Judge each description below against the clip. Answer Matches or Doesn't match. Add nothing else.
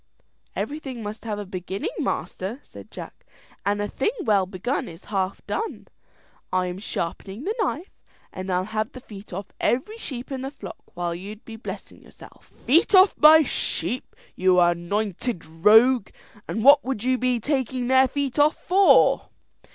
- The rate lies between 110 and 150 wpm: Doesn't match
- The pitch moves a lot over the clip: Matches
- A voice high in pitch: Matches